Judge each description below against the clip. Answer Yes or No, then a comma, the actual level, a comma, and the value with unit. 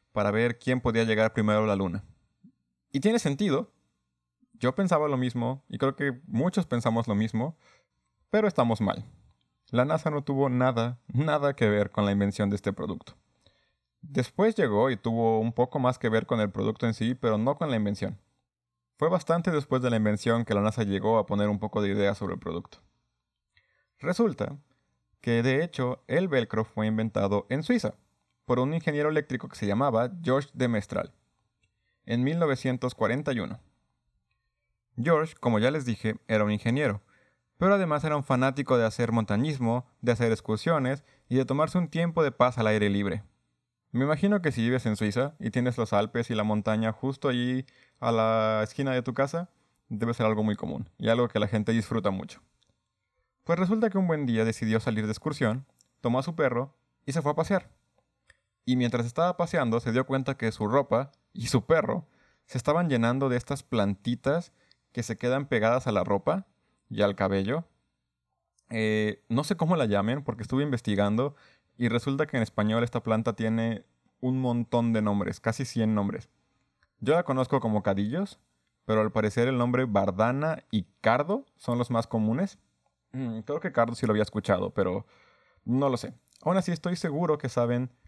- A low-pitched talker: Yes, low, 120 Hz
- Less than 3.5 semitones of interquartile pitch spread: No, average, 4.2 semitones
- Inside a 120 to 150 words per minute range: No, average, 185 wpm